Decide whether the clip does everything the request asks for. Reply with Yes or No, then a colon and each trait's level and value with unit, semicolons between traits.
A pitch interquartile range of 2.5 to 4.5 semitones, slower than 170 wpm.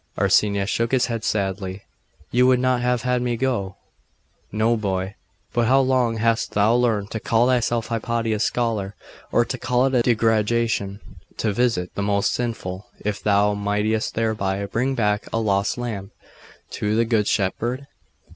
Yes: average, 2.9 semitones; average, 160 wpm